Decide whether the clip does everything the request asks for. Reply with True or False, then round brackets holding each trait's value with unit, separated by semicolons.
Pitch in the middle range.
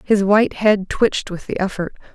False (200 Hz)